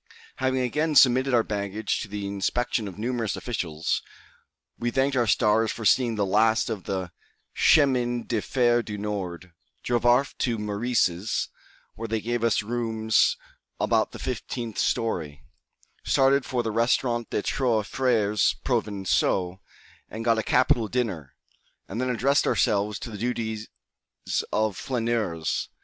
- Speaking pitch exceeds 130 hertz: No, low, 115 Hz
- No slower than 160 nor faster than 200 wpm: No, average, 140 wpm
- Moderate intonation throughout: Yes, average, 3.0 semitones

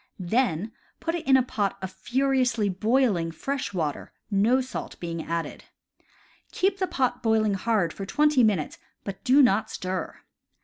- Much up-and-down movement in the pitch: Yes, wide, 5.7 semitones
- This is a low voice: No, high, 220 Hz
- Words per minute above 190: No, average, 150 wpm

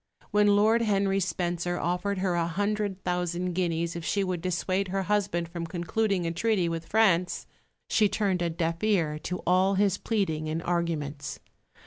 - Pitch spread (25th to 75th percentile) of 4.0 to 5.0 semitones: No, average, 2.9 semitones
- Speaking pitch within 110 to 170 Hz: No, medium, 180 Hz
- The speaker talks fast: No, average, 165 wpm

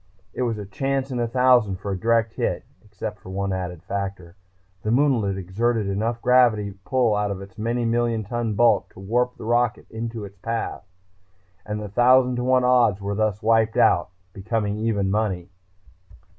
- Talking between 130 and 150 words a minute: No, average, 180 wpm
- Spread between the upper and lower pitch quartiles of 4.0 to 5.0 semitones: No, average, 3.2 semitones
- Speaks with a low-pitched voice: Yes, low, 110 Hz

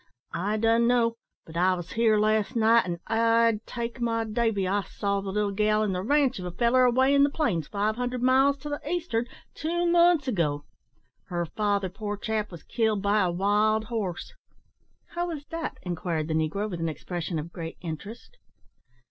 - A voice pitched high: Yes, high, 215 Hz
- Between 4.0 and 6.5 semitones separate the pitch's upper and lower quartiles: Yes, average, 4.5 semitones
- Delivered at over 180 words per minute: Yes, average, 190 wpm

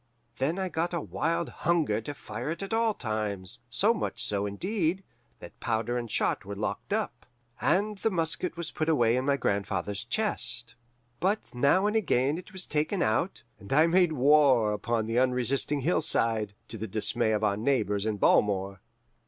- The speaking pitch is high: No, low, 130 Hz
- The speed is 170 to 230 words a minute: Yes, average, 175 wpm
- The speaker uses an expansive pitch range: Yes, wide, 7.8 semitones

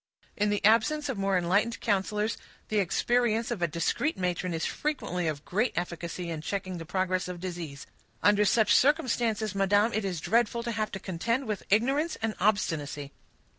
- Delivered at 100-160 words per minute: No, average, 170 wpm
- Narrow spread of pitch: No, average, 4.3 semitones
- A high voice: Yes, high, 205 Hz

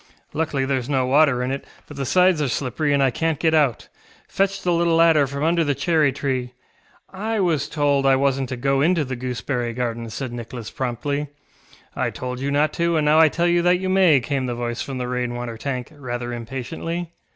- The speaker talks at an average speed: No, fast, 215 wpm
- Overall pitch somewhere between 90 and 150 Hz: Yes, medium, 140 Hz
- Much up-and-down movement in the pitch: No, average, 4.3 semitones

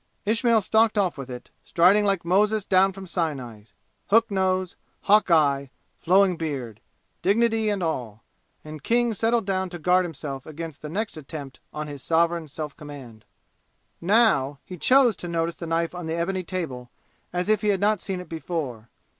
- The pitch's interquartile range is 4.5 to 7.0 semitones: Yes, average, 4.8 semitones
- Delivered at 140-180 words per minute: Yes, average, 170 wpm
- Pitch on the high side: No, medium, 175 Hz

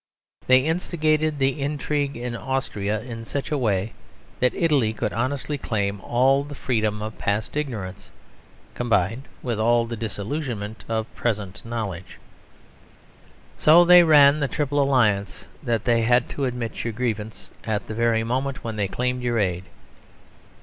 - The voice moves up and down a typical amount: Yes, average, 4.2 semitones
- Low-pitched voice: Yes, low, 120 Hz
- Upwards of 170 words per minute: No, average, 150 wpm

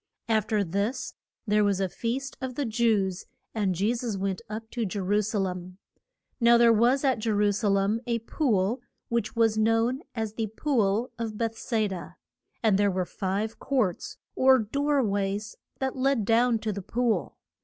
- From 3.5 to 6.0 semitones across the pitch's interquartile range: No, average, 2.9 semitones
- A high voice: Yes, high, 220 Hz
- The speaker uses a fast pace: No, average, 185 wpm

